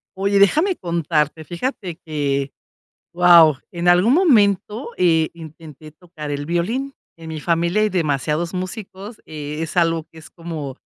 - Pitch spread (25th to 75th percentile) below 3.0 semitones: No, average, 3.8 semitones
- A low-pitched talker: No, medium, 170 Hz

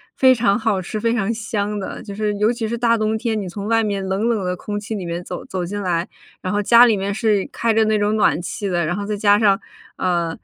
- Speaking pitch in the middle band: No, high, 205 Hz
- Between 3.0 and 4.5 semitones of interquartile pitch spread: No, narrow, 2.4 semitones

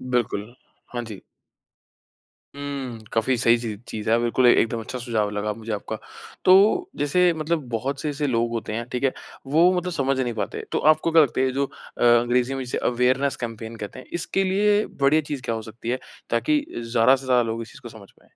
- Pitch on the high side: No, low, 125 Hz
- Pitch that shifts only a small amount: No, average, 3.7 semitones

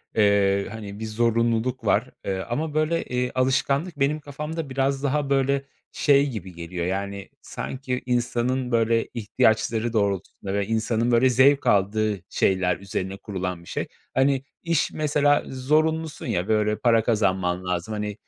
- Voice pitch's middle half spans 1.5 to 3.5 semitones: No, average, 5.1 semitones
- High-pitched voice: No, low, 115 Hz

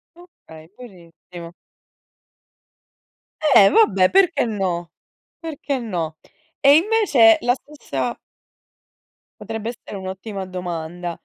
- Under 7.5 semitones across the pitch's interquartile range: No, wide, 8.1 semitones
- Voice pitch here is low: No, high, 210 Hz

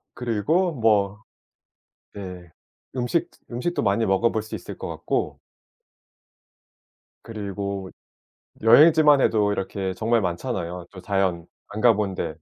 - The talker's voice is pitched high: No, low, 105 Hz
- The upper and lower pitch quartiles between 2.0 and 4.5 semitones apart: Yes, average, 3.6 semitones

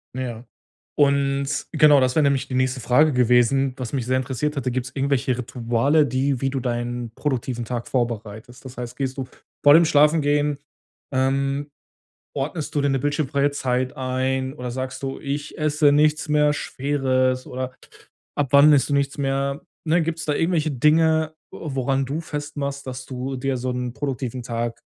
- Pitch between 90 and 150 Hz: Yes, low, 135 Hz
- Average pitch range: No, narrow, 2.3 semitones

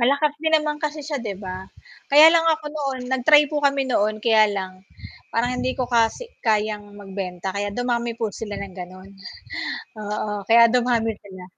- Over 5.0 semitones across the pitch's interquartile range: Yes, wide, 5.5 semitones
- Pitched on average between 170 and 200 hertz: No, high, 230 Hz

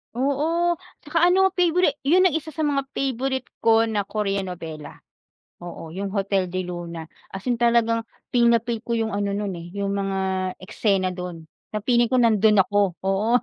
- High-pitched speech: Yes, high, 220 Hz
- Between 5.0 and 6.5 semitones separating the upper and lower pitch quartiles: Yes, wide, 5.4 semitones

